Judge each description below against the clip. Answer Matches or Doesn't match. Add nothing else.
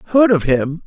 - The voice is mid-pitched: Matches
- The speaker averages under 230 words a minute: Matches